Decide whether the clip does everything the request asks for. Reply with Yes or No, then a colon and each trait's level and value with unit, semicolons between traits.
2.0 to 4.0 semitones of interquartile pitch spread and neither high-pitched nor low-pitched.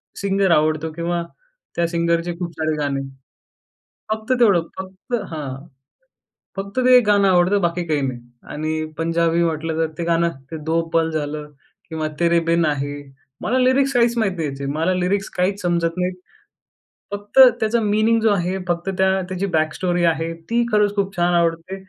Yes: average, 3.6 semitones; medium, 170 Hz